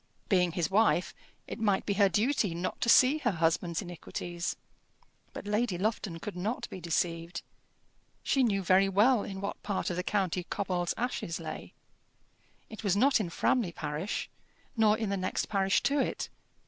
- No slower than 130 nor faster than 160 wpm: No, average, 170 wpm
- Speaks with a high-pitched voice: Yes, high, 195 Hz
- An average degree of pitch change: Yes, average, 3.7 semitones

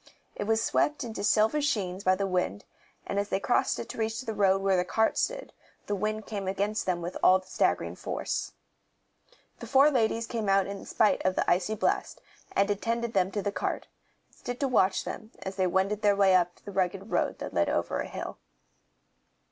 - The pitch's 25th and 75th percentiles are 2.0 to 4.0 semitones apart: Yes, average, 2.7 semitones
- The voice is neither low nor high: No, high, 200 Hz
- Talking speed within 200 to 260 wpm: Yes, fast, 205 wpm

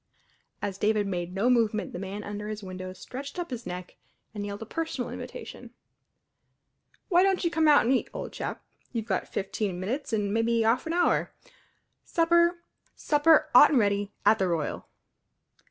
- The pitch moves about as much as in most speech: No, wide, 6.3 semitones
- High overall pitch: Yes, high, 220 Hz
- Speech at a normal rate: Yes, average, 170 wpm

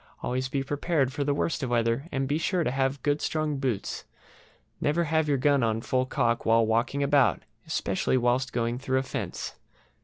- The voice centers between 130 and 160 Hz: Yes, low, 135 Hz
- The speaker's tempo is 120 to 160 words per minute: No, average, 190 wpm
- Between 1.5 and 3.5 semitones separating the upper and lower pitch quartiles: Yes, average, 3.0 semitones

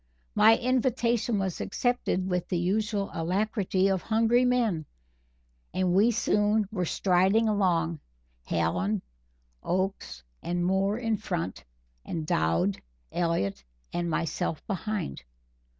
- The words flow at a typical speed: No, slow, 110 wpm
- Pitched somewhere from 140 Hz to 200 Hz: Yes, high, 190 Hz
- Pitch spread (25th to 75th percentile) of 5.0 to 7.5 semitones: No, average, 4.4 semitones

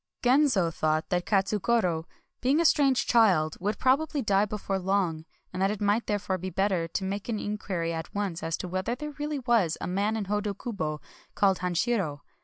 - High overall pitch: Yes, high, 200 Hz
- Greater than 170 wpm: Yes, average, 185 wpm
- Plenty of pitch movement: No, average, 4.4 semitones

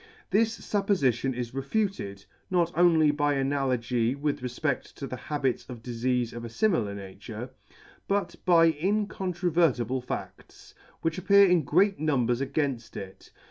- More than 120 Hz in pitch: Yes, medium, 140 Hz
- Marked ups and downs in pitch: Yes, wide, 6.3 semitones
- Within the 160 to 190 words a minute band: No, average, 140 wpm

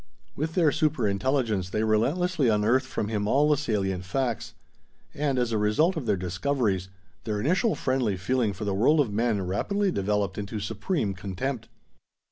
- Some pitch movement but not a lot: No, wide, 5.8 semitones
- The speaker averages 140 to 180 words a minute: Yes, average, 165 wpm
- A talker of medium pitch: No, low, 110 Hz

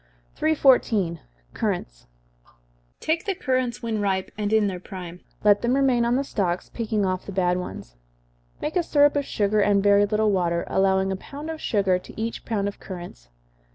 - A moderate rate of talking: Yes, average, 180 wpm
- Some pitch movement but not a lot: Yes, average, 4.7 semitones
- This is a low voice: No, high, 205 Hz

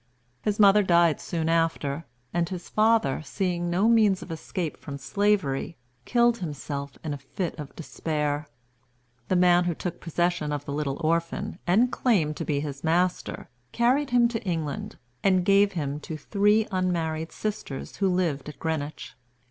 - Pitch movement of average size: Yes, average, 4.7 semitones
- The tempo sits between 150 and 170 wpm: Yes, average, 160 wpm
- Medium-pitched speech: Yes, medium, 170 Hz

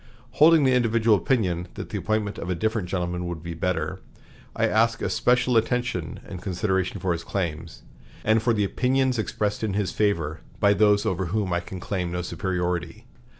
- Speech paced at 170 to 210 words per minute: Yes, average, 180 wpm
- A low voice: Yes, low, 100 Hz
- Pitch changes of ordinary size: Yes, average, 3.9 semitones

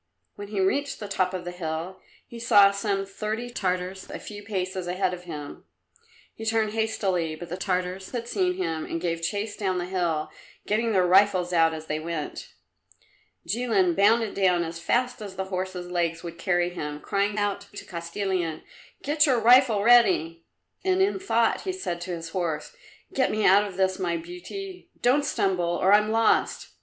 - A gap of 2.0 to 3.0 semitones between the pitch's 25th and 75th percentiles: No, average, 3.8 semitones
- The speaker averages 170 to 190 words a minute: Yes, average, 180 wpm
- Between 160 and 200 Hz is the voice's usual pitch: Yes, high, 190 Hz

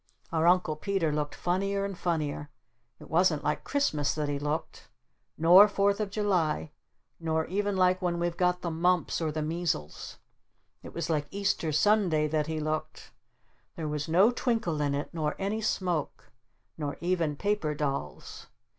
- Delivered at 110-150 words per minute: No, average, 160 wpm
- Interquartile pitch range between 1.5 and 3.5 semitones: No, average, 4.1 semitones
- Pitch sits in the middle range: Yes, medium, 170 Hz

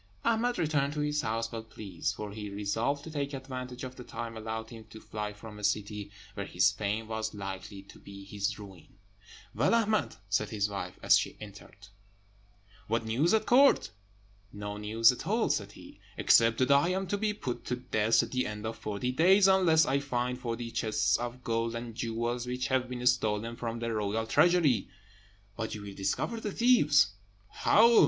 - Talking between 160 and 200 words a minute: Yes, average, 190 wpm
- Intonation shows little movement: No, average, 4.9 semitones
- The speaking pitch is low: Yes, low, 115 Hz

